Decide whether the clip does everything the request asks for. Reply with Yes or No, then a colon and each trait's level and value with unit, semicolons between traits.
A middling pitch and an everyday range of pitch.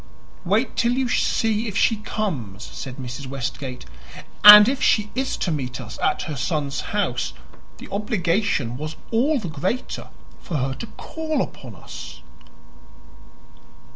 No: medium, 175 Hz; wide, 8.8 semitones